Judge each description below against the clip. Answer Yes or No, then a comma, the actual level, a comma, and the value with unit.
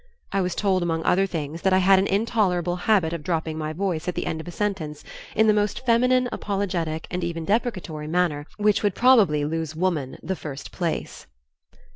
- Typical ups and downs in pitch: Yes, average, 3.9 semitones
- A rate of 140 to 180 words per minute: No, average, 195 wpm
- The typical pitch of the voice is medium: Yes, medium, 180 Hz